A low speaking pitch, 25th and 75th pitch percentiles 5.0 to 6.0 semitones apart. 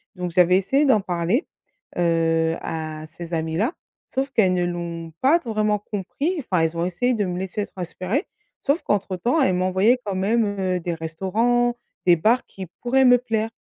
No: high, 190 Hz; wide, 5.6 semitones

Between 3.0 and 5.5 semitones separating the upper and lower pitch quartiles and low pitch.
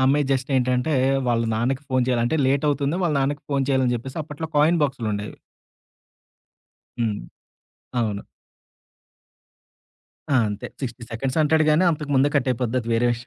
Yes: average, 3.3 semitones; low, 130 Hz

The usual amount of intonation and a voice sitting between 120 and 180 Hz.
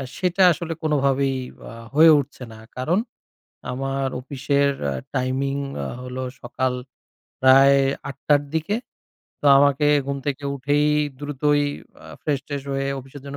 No: narrow, 1.7 semitones; medium, 140 Hz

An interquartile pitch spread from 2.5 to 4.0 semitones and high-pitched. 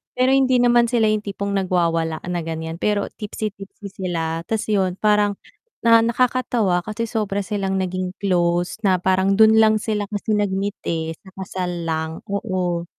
Yes: average, 3.3 semitones; high, 195 Hz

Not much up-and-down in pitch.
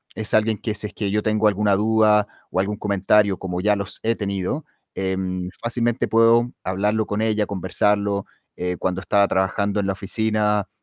Yes: narrow, 1.9 semitones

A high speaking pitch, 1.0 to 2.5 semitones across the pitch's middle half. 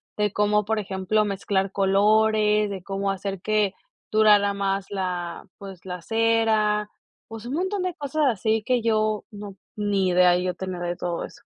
Yes: high, 205 Hz; narrow, 2.1 semitones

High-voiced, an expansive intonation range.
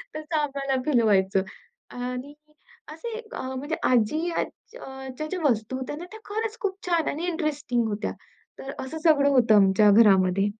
Yes: very high, 270 Hz; wide, 6.0 semitones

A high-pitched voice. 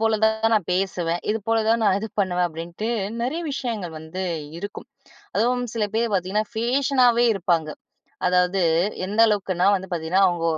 Yes: high, 200 Hz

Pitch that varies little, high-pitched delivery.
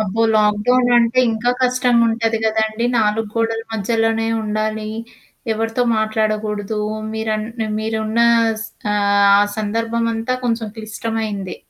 Yes: narrow, 1.1 semitones; high, 220 Hz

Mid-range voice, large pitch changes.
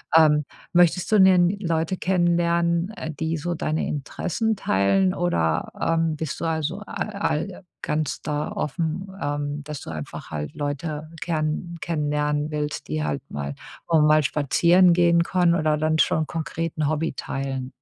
No: medium, 160 Hz; average, 2.7 semitones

